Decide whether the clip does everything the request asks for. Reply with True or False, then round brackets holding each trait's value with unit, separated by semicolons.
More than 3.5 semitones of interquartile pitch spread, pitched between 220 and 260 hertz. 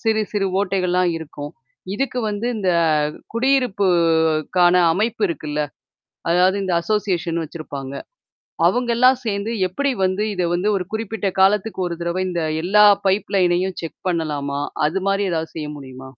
False (4.2 semitones; 185 Hz)